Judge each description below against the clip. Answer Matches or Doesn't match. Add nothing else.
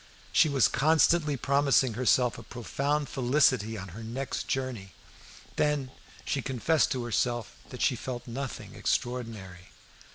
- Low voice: Matches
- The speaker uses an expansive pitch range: Doesn't match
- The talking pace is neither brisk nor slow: Doesn't match